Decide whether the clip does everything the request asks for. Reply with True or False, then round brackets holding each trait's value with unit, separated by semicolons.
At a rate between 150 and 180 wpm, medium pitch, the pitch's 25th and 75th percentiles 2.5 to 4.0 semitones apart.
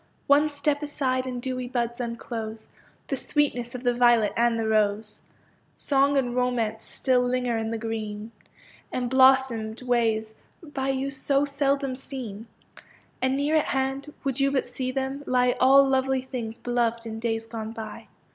False (155 wpm; 250 Hz; 2.9 semitones)